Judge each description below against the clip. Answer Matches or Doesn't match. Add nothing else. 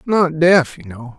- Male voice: Matches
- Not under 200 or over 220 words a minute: Matches